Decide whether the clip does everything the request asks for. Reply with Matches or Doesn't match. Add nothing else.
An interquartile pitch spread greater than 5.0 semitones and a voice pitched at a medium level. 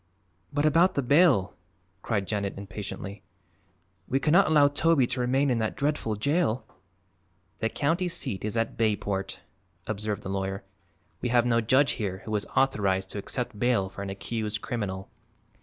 Doesn't match